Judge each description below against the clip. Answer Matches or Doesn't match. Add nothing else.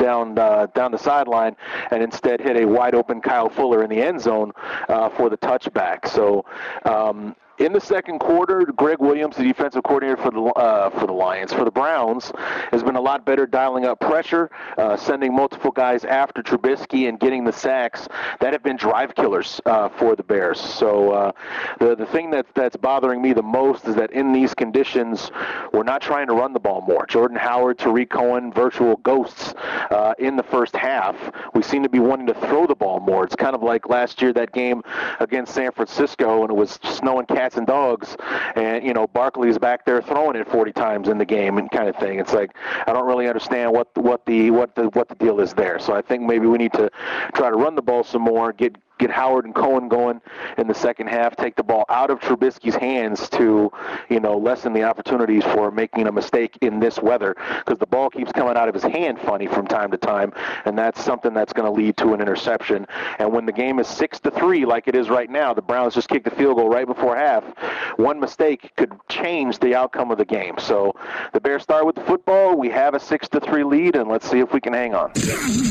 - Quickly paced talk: Matches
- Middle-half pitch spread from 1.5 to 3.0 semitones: Matches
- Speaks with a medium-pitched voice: Doesn't match